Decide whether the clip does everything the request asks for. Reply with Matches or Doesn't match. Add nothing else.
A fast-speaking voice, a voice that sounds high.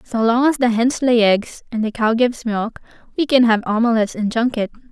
Matches